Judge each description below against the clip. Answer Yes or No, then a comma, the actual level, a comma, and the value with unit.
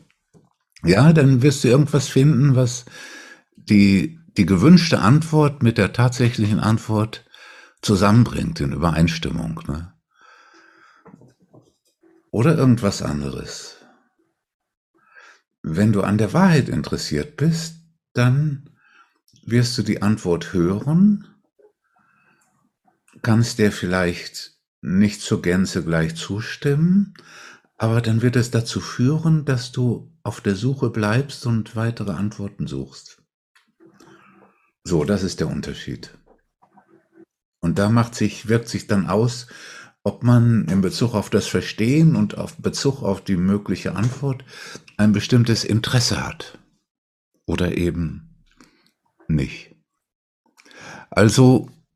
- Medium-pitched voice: No, low, 115 Hz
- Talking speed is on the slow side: Yes, slow, 110 wpm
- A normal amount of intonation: No, wide, 6.0 semitones